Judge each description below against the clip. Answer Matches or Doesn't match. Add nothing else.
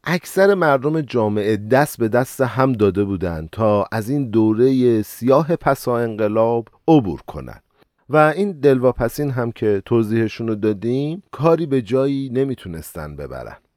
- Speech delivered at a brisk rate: Doesn't match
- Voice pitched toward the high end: Doesn't match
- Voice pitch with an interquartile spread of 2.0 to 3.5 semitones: Doesn't match